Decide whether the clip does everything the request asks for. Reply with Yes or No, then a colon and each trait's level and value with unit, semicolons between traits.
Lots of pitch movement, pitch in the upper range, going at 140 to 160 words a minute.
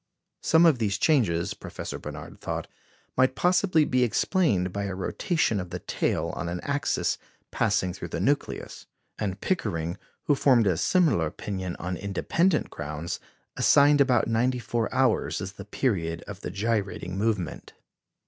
No: wide, 6.8 semitones; low, 105 Hz; average, 150 wpm